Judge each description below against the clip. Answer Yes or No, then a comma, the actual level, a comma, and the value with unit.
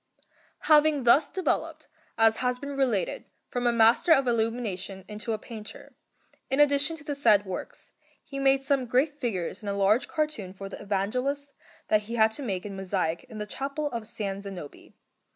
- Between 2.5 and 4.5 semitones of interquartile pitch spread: No, wide, 5.5 semitones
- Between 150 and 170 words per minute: No, average, 180 wpm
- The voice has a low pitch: No, high, 230 Hz